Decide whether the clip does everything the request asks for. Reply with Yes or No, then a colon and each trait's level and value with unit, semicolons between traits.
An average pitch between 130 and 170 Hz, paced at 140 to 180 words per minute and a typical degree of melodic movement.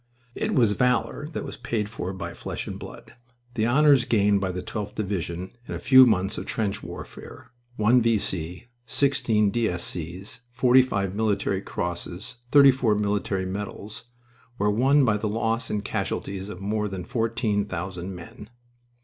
No: low, 105 Hz; average, 165 wpm; average, 3.4 semitones